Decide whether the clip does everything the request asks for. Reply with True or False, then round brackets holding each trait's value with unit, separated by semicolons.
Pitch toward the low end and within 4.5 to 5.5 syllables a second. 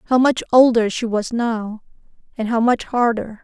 False (230 Hz; 4.6 syllables/s)